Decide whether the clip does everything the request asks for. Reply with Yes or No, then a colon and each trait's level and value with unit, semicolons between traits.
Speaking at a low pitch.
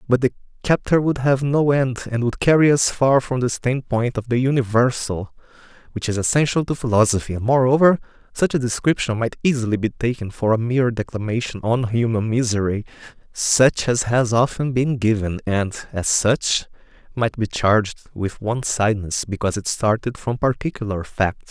Yes: low, 120 Hz